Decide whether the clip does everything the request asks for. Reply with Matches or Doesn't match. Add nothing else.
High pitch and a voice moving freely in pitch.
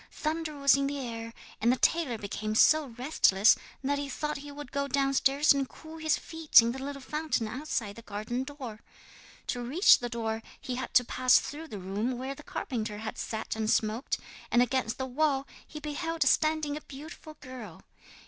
Doesn't match